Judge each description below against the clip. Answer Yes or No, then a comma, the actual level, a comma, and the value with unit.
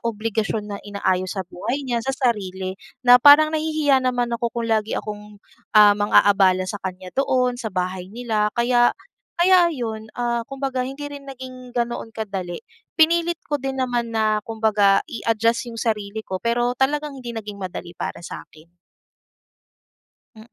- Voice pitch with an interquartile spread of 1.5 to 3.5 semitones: No, average, 3.9 semitones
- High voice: Yes, high, 230 Hz